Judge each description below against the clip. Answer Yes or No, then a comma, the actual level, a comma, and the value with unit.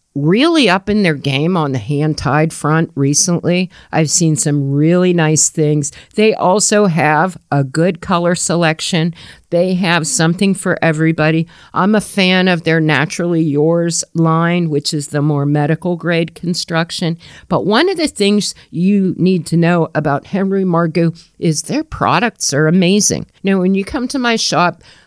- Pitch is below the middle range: No, medium, 170 Hz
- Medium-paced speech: Yes, average, 165 wpm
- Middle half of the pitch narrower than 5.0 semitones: Yes, average, 3.1 semitones